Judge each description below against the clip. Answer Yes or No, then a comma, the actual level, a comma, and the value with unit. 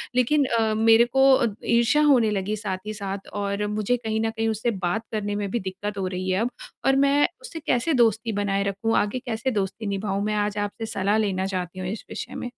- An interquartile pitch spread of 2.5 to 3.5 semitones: Yes, average, 2.9 semitones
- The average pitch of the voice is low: No, high, 215 Hz